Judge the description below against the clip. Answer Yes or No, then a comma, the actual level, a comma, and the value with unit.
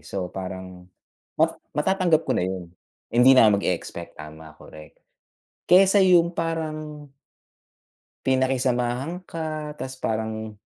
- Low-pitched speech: Yes, low, 130 Hz